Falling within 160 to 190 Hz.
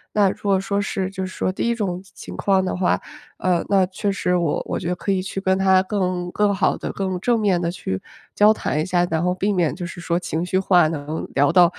Yes: medium, 185 Hz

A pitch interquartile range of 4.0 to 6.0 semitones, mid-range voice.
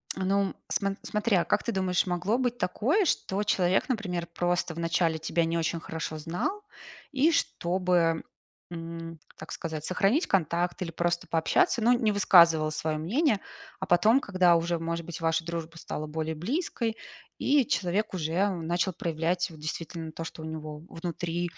No: average, 3.2 semitones; medium, 175 Hz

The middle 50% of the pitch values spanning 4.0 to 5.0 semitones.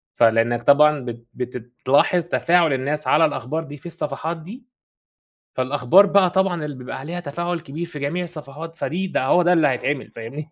Yes: average, 4.7 semitones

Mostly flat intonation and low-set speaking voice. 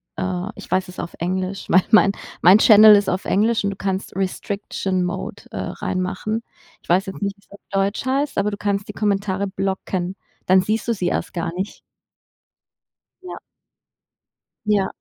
No: narrow, 1.7 semitones; high, 195 Hz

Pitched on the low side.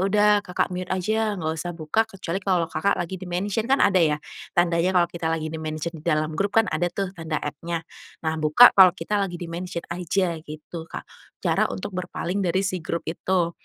No: medium, 175 Hz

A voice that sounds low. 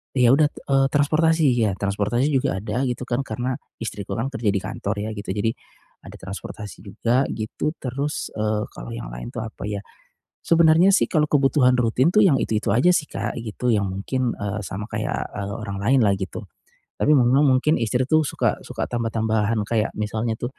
Yes: low, 115 Hz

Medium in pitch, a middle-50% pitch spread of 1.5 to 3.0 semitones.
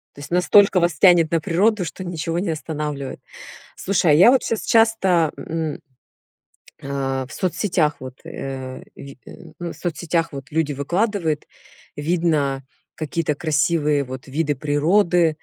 No: medium, 160 Hz; average, 3.5 semitones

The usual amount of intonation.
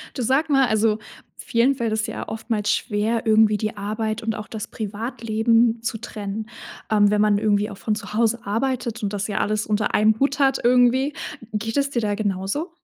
No: narrow, 2.1 semitones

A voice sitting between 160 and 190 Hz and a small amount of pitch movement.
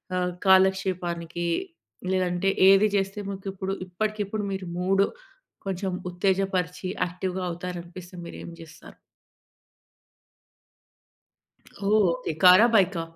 Yes: medium, 185 Hz; narrow, 1.6 semitones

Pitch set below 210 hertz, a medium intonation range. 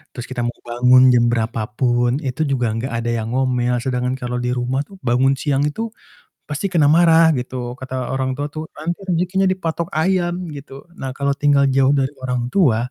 Yes: low, 135 Hz; average, 4.2 semitones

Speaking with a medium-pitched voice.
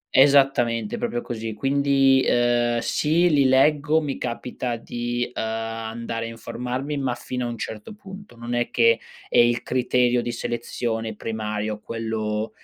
No: low, 120 Hz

